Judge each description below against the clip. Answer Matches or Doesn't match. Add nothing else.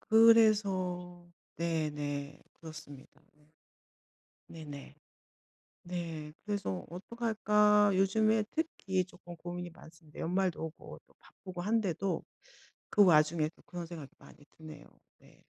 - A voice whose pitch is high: Doesn't match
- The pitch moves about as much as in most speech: Matches